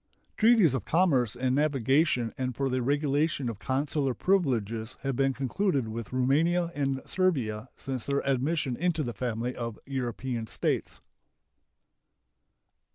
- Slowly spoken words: Yes, slow, 130 wpm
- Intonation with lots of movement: No, average, 3.6 semitones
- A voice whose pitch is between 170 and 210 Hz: No, low, 135 Hz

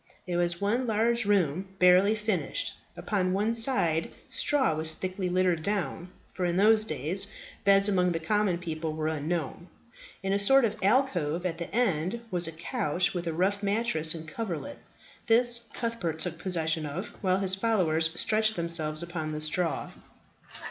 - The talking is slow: No, average, 160 wpm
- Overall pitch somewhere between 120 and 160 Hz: No, medium, 185 Hz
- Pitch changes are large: No, average, 4.3 semitones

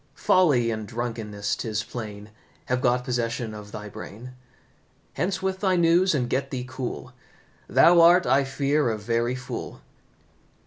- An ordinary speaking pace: Yes, average, 145 wpm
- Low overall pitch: Yes, low, 125 Hz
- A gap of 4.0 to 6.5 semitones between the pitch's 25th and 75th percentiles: Yes, average, 4.4 semitones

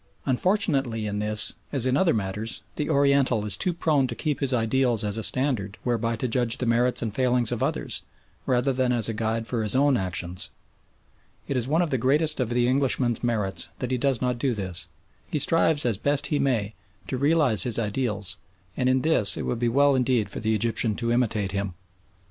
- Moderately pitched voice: No, low, 120 Hz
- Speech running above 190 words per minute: Yes, fast, 205 wpm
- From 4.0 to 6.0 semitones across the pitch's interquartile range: No, average, 3.6 semitones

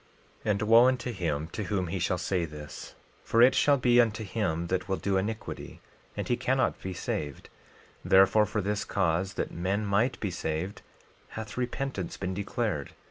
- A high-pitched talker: No, low, 100 Hz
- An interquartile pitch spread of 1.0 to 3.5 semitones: No, average, 3.9 semitones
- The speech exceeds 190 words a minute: No, average, 180 wpm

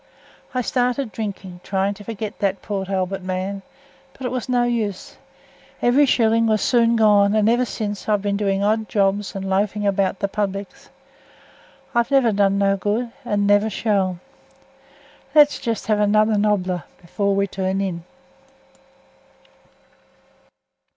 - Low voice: No, high, 205 Hz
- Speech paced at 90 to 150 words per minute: Yes, average, 140 wpm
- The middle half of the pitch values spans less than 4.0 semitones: Yes, narrow, 2.5 semitones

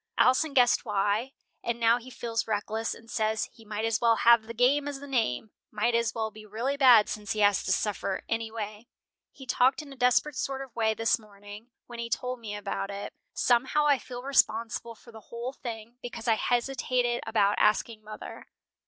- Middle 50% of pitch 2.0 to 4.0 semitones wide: Yes, narrow, 2.5 semitones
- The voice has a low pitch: No, high, 230 Hz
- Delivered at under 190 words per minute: No, average, 195 wpm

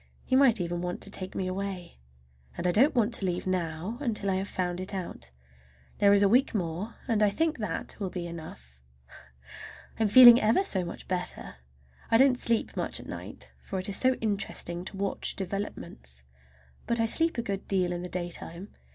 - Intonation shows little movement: No, average, 4.1 semitones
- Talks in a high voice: Yes, high, 195 Hz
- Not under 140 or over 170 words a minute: No, average, 195 wpm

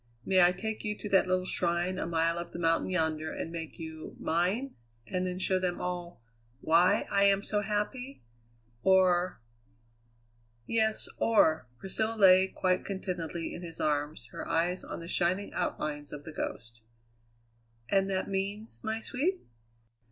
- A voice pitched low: No, medium, 180 Hz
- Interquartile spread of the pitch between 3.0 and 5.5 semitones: Yes, average, 3.4 semitones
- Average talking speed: Yes, average, 160 wpm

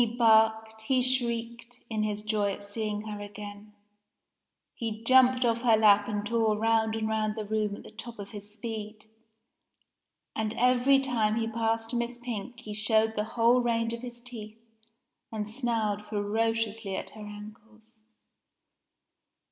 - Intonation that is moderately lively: No, narrow, 1.7 semitones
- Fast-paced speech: No, average, 155 wpm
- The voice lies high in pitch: Yes, high, 220 Hz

